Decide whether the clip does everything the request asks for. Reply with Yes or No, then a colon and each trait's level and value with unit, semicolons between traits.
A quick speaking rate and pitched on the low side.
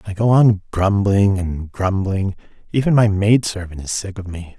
No: average, 170 wpm; low, 100 Hz